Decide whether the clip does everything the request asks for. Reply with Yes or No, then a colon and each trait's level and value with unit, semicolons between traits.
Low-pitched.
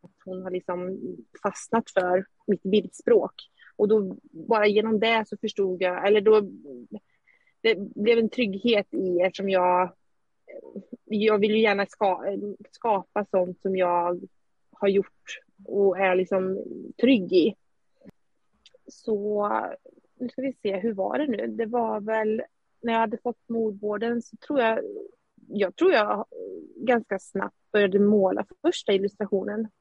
No: high, 210 Hz